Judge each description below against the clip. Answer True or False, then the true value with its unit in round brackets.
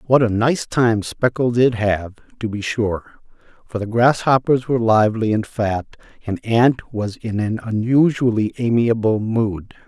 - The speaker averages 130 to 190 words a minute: True (150 wpm)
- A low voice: True (115 Hz)